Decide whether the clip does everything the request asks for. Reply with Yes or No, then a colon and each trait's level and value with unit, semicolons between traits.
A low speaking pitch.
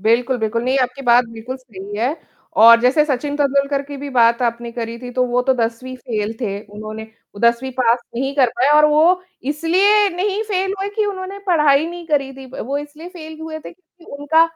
No: very high, 270 Hz